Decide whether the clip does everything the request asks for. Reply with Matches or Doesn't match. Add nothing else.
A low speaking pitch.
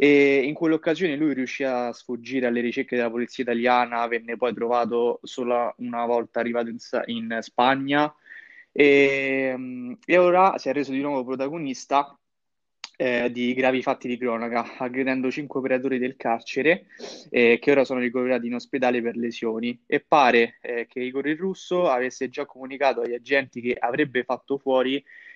Matches